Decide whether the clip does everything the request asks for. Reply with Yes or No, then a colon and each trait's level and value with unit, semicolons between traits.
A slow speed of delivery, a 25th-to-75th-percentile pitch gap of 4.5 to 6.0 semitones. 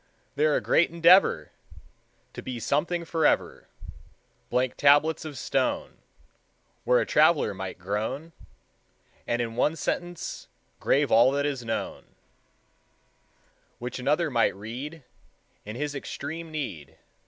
Yes: slow, 120 wpm; average, 5.2 semitones